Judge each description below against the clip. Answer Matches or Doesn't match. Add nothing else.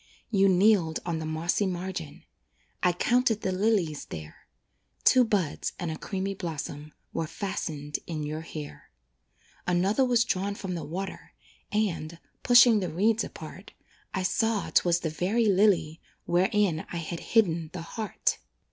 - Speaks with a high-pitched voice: Doesn't match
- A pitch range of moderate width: Matches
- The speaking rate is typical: Matches